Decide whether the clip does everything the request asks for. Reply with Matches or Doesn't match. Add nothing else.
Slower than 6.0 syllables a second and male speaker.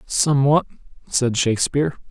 Matches